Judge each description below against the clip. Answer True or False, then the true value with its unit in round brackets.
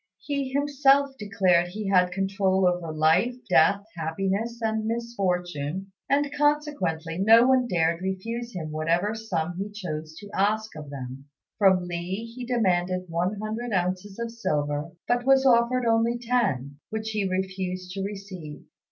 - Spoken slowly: False (145 wpm)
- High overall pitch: True (195 Hz)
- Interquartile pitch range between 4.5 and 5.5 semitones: True (4.8 semitones)